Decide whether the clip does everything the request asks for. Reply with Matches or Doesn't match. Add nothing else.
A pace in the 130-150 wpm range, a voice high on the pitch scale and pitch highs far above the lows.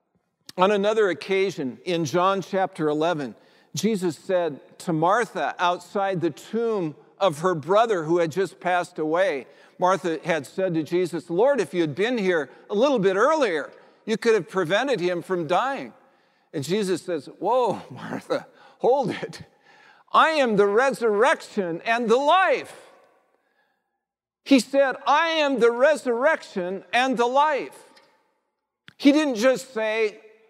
Matches